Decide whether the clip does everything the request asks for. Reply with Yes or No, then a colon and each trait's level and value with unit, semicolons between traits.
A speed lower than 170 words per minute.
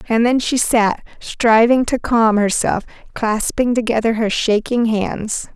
Yes: average, 140 wpm